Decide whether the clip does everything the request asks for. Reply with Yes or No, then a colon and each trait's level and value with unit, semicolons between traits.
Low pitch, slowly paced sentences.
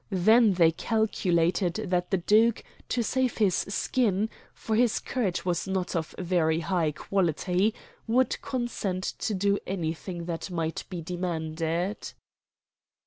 No: medium, 185 Hz; slow, 130 wpm